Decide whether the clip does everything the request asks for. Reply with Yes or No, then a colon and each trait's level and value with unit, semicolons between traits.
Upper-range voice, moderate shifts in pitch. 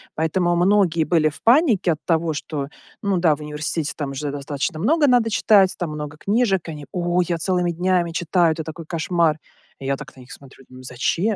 No: medium, 165 Hz; average, 3.5 semitones